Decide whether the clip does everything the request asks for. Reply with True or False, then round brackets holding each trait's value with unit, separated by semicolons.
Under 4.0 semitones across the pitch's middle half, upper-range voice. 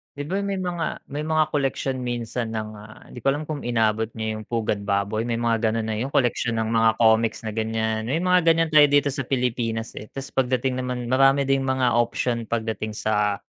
False (3.5 semitones; 120 Hz)